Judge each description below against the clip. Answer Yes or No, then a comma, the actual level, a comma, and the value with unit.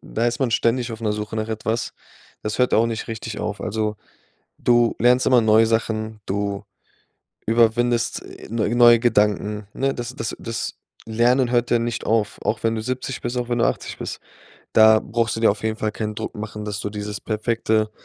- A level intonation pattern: Yes, narrow, 1.8 semitones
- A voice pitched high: No, low, 115 Hz